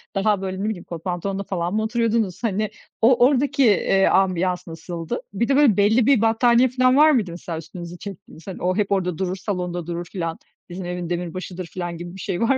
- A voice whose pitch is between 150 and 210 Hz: Yes, high, 190 Hz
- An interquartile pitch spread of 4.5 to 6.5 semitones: No, average, 4.1 semitones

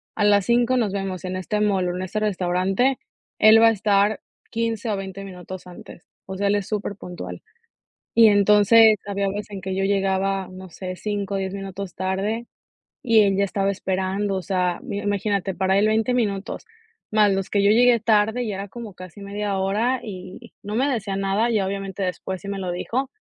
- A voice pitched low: No, high, 200 Hz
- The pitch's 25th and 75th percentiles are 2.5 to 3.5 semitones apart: No, narrow, 2.0 semitones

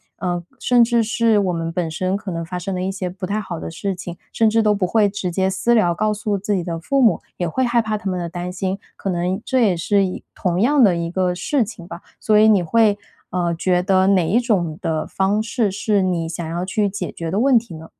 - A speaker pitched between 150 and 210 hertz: Yes, high, 190 Hz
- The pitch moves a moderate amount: Yes, average, 3.4 semitones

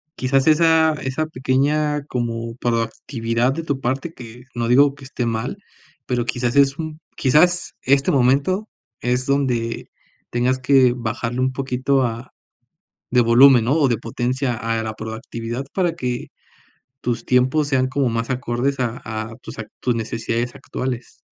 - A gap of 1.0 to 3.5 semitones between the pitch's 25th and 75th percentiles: Yes, average, 2.8 semitones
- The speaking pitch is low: Yes, low, 125 Hz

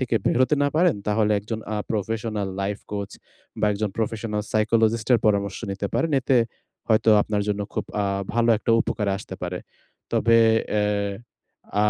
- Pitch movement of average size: No, narrow, 2.1 semitones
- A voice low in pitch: Yes, low, 110 Hz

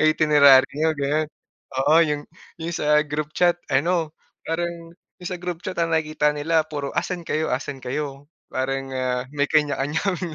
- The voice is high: No, medium, 150 Hz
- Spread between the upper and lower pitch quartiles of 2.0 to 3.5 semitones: Yes, narrow, 2.5 semitones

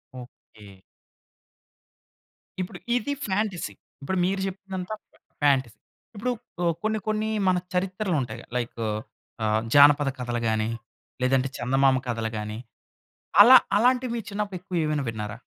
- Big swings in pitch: Yes, wide, 8.7 semitones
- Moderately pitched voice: Yes, medium, 155 Hz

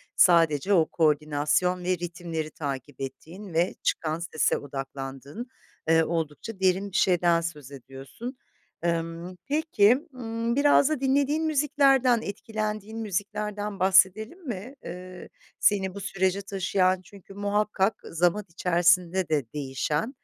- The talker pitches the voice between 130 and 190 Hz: Yes, medium, 185 Hz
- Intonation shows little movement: No, average, 4.6 semitones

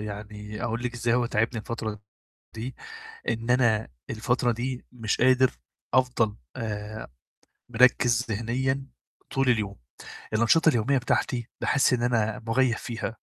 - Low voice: Yes, low, 120 Hz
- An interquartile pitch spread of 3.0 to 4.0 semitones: No, narrow, 2.4 semitones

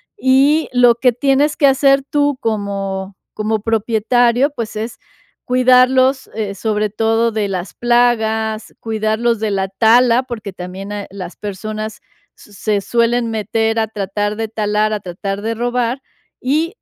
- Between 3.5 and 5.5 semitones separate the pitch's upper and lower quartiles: No, average, 3.0 semitones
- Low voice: No, high, 225 Hz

